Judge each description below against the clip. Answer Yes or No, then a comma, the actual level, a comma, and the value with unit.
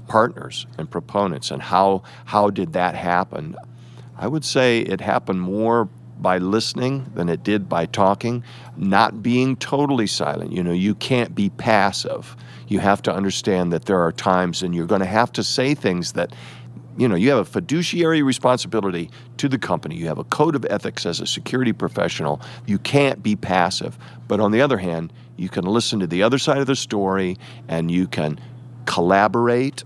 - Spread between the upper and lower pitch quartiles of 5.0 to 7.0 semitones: Yes, wide, 5.6 semitones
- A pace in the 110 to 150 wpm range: No, average, 185 wpm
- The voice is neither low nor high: No, low, 105 Hz